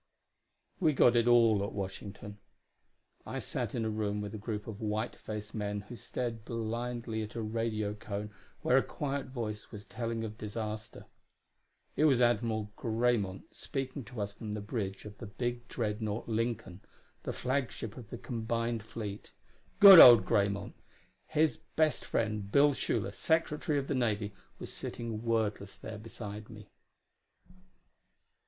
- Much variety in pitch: No, narrow, 2.5 semitones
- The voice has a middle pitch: No, low, 110 Hz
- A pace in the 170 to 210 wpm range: No, average, 150 wpm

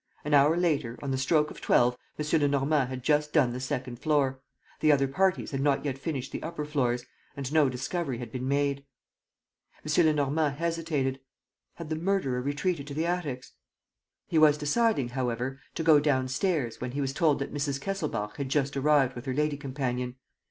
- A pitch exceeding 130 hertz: Yes, medium, 140 Hz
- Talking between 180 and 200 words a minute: Yes, average, 185 wpm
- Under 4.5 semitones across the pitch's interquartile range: Yes, average, 2.7 semitones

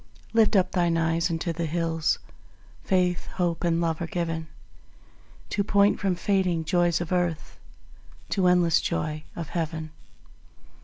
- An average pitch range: No, narrow, 1.8 semitones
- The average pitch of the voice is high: No, medium, 170 Hz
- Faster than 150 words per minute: No, average, 140 wpm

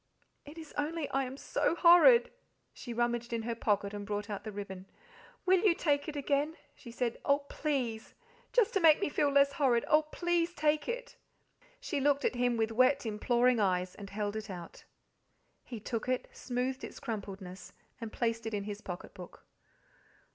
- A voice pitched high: Yes, high, 245 Hz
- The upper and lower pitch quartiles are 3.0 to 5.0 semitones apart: No, wide, 5.6 semitones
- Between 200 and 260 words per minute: No, average, 185 wpm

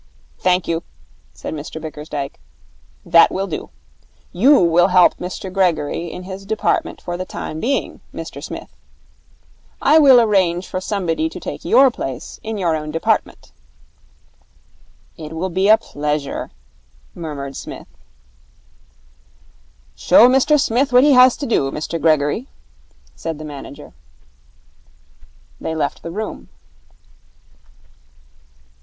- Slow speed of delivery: Yes, slow, 125 wpm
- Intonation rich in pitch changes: Yes, wide, 5.8 semitones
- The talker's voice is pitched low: No, medium, 175 Hz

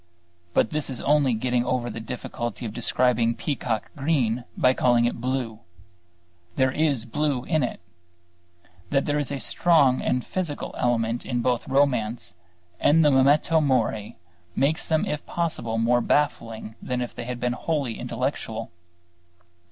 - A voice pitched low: Yes, low, 125 Hz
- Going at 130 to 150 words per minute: Yes, average, 145 wpm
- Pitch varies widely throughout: No, average, 3.5 semitones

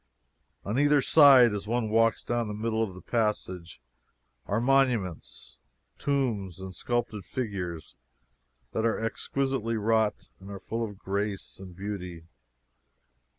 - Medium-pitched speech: No, low, 110 Hz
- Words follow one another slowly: Yes, slow, 130 wpm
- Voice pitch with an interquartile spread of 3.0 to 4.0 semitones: Yes, average, 3.6 semitones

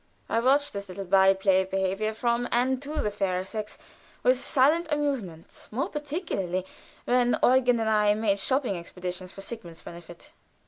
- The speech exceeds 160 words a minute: Yes, average, 170 wpm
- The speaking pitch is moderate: No, high, 215 Hz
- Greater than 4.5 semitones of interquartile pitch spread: Yes, average, 5.2 semitones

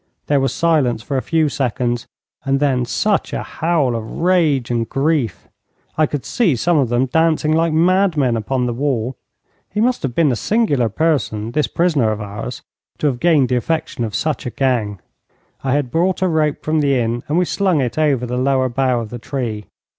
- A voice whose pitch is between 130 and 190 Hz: Yes, low, 135 Hz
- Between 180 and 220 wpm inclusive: Yes, fast, 205 wpm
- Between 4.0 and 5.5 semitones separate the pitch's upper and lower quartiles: Yes, average, 4.7 semitones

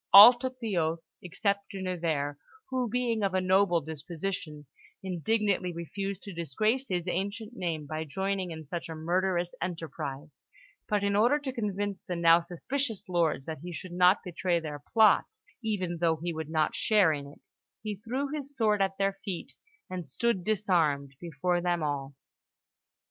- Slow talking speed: No, average, 165 wpm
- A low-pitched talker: No, medium, 180 Hz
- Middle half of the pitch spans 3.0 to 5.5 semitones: Yes, average, 4.1 semitones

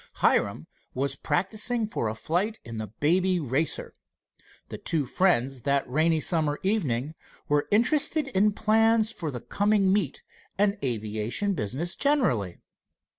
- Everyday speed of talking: No, slow, 130 wpm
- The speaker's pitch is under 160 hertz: No, medium, 165 Hz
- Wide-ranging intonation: Yes, wide, 8.1 semitones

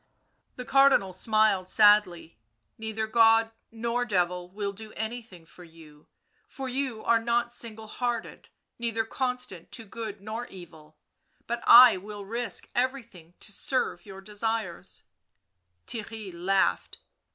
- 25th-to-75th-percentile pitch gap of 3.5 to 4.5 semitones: Yes, average, 3.8 semitones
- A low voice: No, high, 220 Hz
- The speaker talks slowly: Yes, slow, 130 wpm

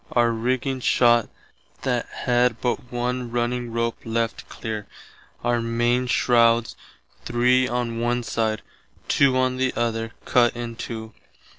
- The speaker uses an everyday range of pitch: No, narrow, 1.1 semitones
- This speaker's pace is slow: Yes, slow, 125 wpm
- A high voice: No, low, 120 Hz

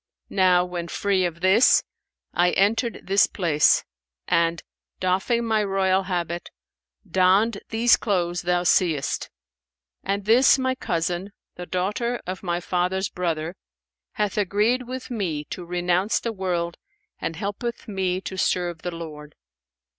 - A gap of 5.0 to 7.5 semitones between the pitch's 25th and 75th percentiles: No, average, 2.8 semitones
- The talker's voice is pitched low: No, medium, 185 Hz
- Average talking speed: No, slow, 130 wpm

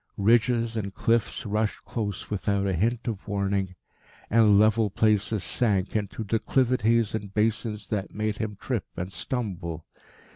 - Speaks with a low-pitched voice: Yes, low, 105 Hz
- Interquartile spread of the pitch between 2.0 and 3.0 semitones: Yes, narrow, 2.4 semitones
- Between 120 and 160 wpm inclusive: Yes, average, 140 wpm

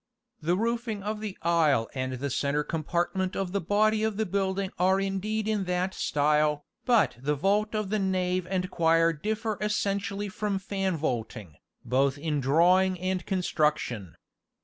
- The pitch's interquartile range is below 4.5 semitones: No, average, 5.0 semitones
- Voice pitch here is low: No, medium, 185 Hz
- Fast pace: No, average, 155 wpm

